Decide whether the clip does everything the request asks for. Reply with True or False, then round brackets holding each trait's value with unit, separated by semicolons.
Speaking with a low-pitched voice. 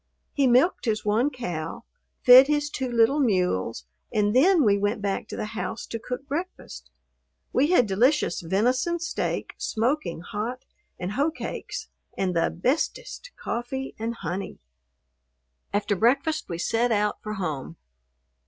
False (235 Hz)